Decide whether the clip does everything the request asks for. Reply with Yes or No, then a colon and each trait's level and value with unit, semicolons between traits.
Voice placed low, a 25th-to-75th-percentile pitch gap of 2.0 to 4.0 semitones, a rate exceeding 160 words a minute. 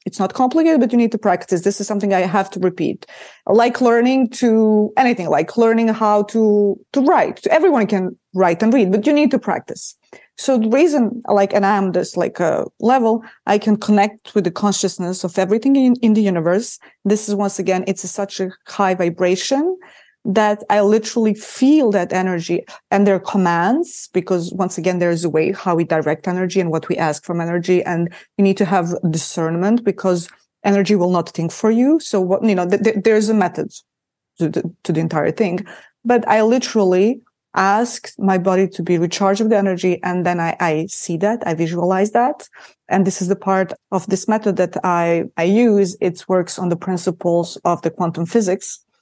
No: high, 195 Hz; average, 3.5 semitones; fast, 205 wpm